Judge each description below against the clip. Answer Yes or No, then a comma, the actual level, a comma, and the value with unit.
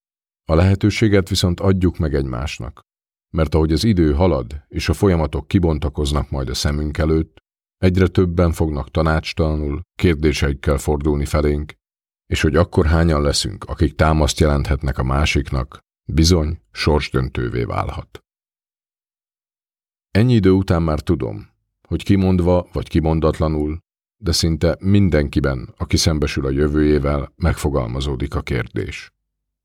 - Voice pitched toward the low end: Yes, very low, 80 Hz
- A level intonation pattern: No, average, 3.4 semitones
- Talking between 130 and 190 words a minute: No, average, 115 wpm